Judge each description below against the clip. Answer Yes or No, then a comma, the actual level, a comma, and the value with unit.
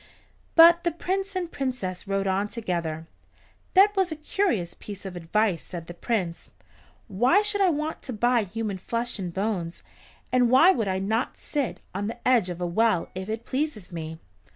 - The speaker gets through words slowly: No, average, 180 wpm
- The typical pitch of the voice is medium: No, high, 220 Hz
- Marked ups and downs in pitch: Yes, wide, 7.8 semitones